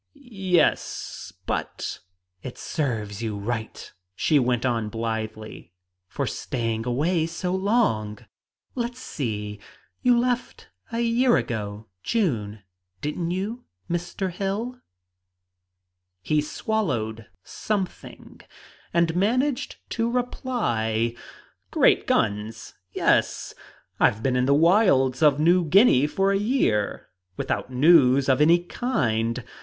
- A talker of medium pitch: Yes, medium, 150 Hz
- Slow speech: Yes, slow, 110 wpm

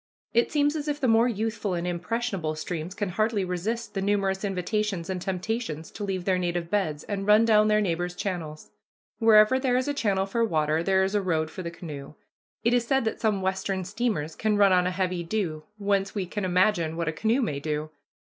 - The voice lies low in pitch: No, high, 195 Hz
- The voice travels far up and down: No, average, 3.8 semitones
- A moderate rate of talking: No, fast, 215 wpm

